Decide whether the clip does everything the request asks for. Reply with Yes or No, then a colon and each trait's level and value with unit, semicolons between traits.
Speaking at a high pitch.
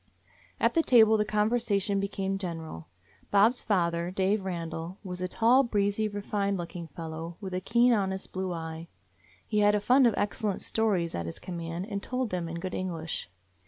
Yes: high, 195 Hz